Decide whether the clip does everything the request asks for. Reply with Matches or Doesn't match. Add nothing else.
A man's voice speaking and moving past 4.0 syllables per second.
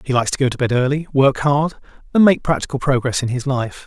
Matches